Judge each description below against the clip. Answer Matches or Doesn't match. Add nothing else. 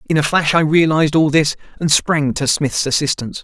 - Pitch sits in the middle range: Matches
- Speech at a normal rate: Doesn't match